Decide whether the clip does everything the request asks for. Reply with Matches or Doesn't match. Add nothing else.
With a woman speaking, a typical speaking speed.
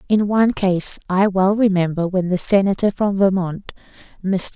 Matches